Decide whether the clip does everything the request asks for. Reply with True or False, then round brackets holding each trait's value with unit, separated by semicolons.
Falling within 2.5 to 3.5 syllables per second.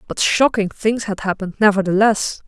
False (5.4 syllables/s)